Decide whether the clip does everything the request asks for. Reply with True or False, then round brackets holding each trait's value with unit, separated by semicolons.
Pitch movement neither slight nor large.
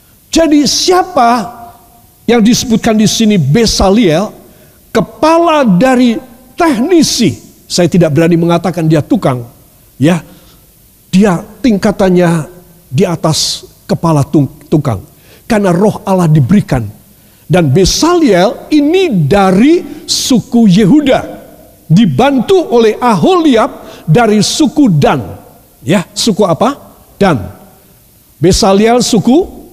False (7.0 semitones)